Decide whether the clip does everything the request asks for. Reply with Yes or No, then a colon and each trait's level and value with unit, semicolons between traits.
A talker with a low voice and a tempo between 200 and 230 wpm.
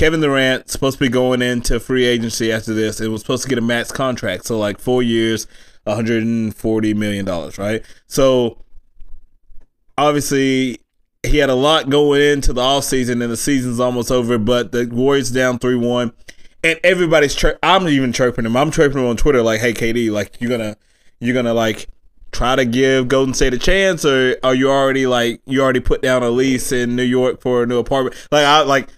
Yes: low, 125 Hz; fast, 205 wpm